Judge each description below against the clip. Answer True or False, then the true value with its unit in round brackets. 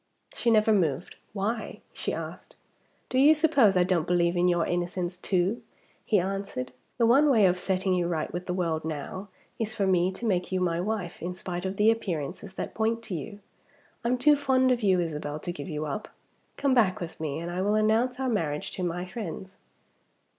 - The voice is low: False (185 Hz)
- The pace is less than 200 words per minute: False (205 wpm)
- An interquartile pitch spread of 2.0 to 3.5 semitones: False (4.1 semitones)